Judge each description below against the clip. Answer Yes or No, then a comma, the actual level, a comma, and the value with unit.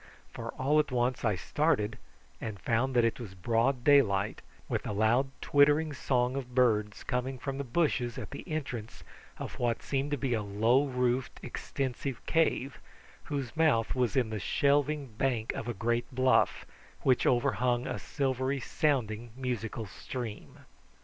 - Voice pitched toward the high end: No, low, 125 Hz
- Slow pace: No, average, 155 wpm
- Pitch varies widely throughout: No, average, 3.1 semitones